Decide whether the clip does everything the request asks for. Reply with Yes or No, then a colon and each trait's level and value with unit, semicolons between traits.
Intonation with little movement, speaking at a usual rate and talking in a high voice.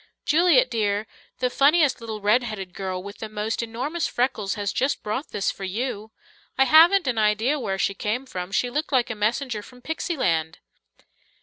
No: average, 4.4 semitones; average, 185 wpm; high, 230 Hz